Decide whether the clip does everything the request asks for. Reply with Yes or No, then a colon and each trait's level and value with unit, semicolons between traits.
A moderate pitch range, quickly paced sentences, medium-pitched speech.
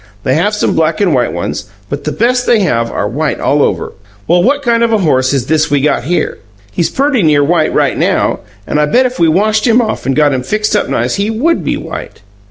No: wide, 7.4 semitones; fast, 245 wpm; medium, 170 Hz